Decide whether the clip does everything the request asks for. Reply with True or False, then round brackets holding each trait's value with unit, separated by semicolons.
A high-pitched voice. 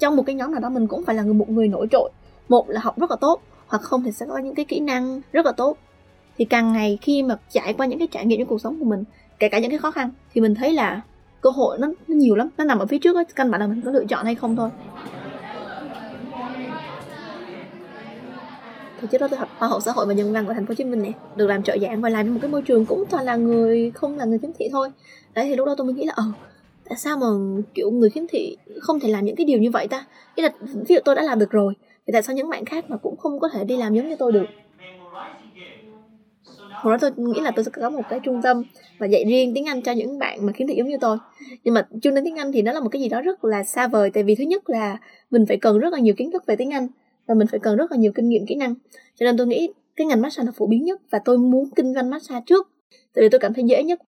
True (245 Hz)